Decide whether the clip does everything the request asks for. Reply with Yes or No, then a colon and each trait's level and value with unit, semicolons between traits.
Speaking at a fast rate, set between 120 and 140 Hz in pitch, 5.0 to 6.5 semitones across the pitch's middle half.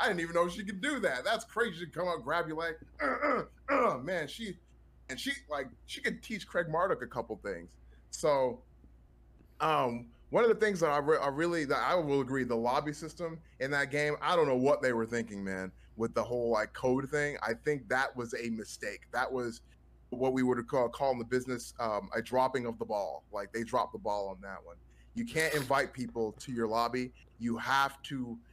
Yes: fast, 225 wpm; low, 130 Hz; wide, 5.5 semitones